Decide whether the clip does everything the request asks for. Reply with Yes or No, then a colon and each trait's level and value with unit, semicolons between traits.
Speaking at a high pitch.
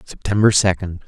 No: very low, 95 Hz